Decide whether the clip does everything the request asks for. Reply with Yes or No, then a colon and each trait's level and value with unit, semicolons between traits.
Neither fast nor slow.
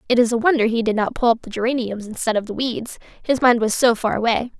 No: fast, 250 wpm